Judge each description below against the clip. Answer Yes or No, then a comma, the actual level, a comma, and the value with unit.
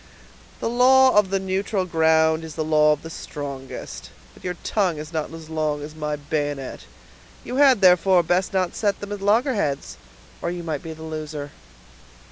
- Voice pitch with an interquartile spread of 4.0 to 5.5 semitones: Yes, average, 4.3 semitones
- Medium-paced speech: Yes, average, 180 wpm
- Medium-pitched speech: Yes, medium, 160 Hz